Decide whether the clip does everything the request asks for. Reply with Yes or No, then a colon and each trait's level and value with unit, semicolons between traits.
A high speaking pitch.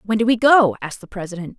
Yes: high, 210 Hz